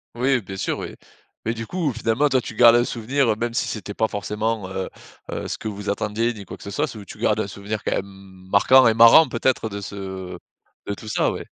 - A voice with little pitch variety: No, average, 3.0 semitones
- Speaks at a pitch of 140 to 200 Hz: No, low, 110 Hz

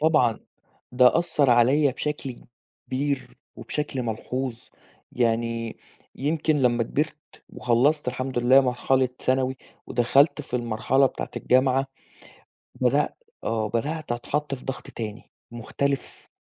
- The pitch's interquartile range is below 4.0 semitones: Yes, average, 2.8 semitones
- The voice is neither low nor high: No, low, 130 Hz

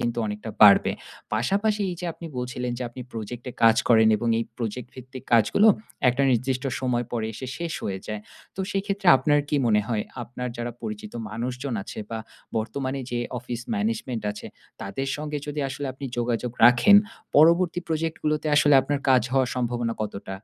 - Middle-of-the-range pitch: No, low, 125 Hz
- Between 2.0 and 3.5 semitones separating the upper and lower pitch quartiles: No, average, 4.3 semitones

